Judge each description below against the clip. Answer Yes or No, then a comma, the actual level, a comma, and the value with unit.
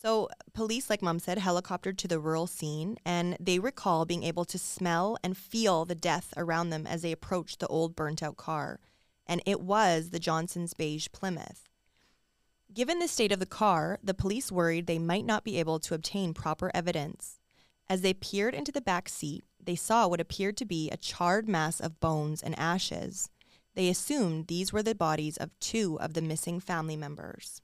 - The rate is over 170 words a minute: Yes, average, 195 wpm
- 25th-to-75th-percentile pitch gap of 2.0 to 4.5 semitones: Yes, average, 3.3 semitones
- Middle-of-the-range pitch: Yes, medium, 175 Hz